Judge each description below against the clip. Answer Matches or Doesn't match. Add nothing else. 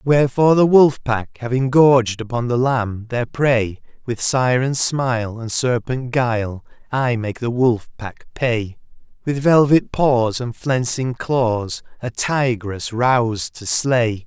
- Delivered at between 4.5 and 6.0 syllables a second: Doesn't match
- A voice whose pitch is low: Matches